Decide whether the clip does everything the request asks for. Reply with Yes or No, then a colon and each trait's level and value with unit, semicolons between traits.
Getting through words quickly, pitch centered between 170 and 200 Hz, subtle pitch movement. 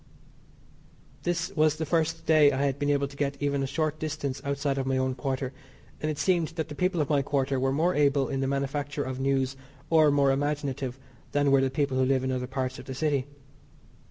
No: fast, 220 wpm; medium, 140 Hz; narrow, 2.1 semitones